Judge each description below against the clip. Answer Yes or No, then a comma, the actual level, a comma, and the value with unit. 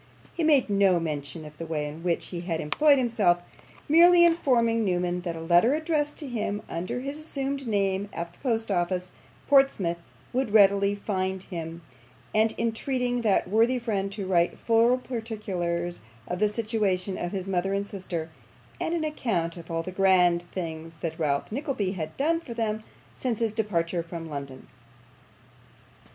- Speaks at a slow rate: No, average, 165 wpm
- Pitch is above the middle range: Yes, high, 195 Hz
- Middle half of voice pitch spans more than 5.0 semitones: Yes, wide, 5.4 semitones